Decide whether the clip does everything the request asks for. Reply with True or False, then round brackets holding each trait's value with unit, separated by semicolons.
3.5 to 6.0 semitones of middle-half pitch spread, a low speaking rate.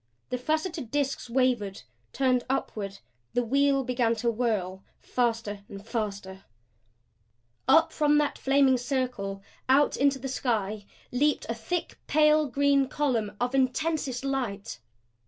True (3.9 semitones; 120 wpm)